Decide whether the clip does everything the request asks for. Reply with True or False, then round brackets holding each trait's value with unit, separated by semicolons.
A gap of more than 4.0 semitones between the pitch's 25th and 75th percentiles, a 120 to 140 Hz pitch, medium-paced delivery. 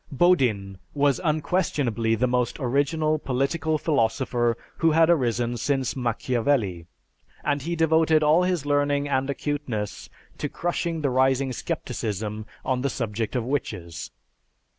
False (4.5 semitones; 135 Hz; 125 wpm)